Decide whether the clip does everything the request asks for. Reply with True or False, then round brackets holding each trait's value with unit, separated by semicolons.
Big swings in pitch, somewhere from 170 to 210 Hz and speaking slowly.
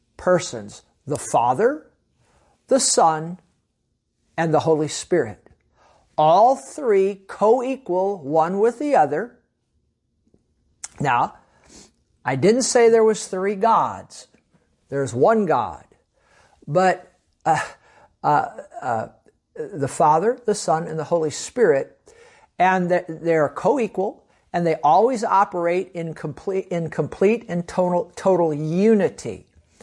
True (5.8 semitones; 185 Hz; 110 wpm)